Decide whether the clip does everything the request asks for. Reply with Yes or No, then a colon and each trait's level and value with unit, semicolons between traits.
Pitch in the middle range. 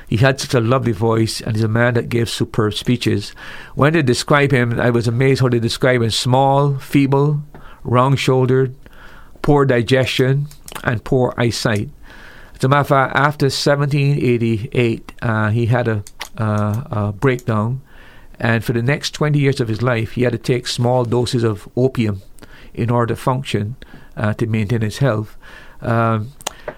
No: low, 125 Hz